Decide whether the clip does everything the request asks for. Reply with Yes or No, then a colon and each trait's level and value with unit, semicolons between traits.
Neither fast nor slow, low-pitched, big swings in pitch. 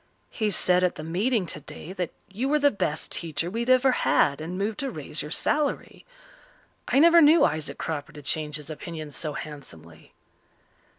No: average, 180 wpm; medium, 170 Hz; wide, 7.7 semitones